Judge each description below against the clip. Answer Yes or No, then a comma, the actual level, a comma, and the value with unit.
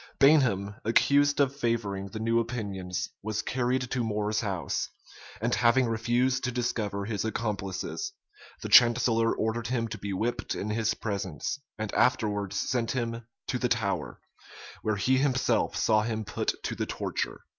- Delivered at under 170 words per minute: Yes, average, 155 wpm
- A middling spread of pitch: Yes, average, 3.0 semitones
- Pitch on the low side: Yes, low, 115 Hz